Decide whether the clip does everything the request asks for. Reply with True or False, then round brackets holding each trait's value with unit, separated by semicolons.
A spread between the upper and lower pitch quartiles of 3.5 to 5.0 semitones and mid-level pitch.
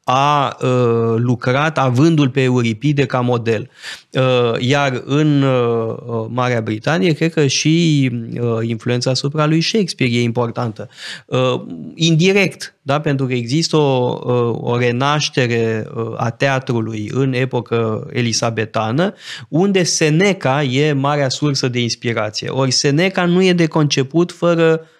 False (4.1 semitones; 130 Hz)